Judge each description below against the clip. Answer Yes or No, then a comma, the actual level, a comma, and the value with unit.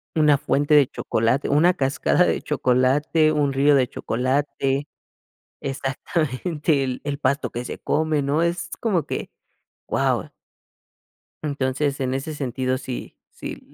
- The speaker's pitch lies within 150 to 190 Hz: No, medium, 140 Hz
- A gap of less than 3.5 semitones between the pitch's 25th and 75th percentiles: Yes, narrow, 2.5 semitones